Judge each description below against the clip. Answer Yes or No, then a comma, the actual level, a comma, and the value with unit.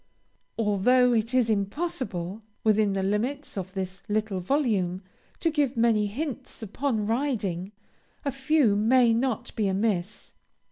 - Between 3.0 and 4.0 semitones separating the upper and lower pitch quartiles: No, average, 4.5 semitones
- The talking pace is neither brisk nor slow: No, slow, 130 wpm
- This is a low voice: No, high, 220 Hz